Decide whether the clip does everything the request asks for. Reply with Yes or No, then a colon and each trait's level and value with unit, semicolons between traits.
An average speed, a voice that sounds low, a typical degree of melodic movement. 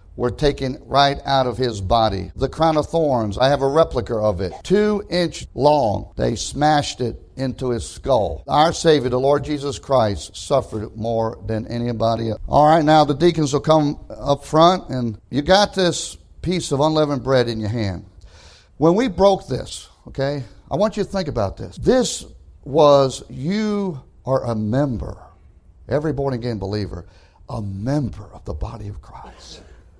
No: average, 170 wpm; low, 130 Hz; wide, 5.9 semitones